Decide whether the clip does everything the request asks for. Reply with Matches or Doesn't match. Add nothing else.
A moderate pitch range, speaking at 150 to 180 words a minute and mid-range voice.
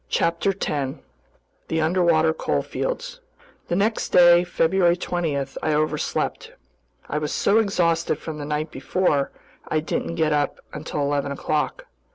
Doesn't match